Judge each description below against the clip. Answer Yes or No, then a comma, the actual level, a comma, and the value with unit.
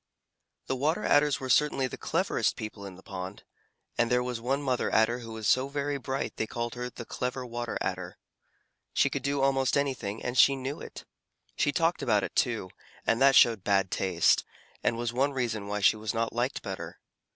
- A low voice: Yes, low, 125 Hz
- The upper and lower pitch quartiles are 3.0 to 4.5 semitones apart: Yes, average, 3.5 semitones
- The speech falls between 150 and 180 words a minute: No, fast, 205 wpm